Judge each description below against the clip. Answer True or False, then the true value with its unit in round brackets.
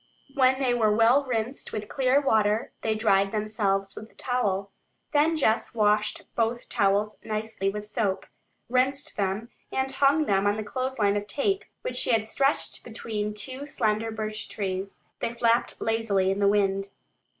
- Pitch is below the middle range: False (220 Hz)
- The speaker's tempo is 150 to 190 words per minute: True (160 wpm)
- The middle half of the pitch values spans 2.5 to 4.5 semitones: True (3.5 semitones)